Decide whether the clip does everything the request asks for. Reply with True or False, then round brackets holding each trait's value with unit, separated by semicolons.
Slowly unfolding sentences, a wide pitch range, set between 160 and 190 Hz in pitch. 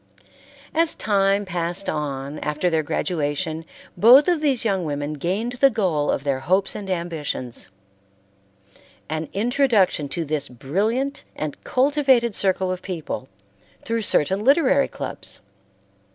True (125 wpm; 7.3 semitones; 185 Hz)